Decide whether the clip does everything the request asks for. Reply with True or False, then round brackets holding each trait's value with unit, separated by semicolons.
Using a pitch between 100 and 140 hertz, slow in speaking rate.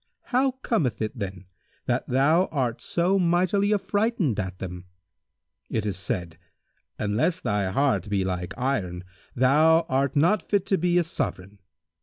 False (135 Hz; 145 wpm)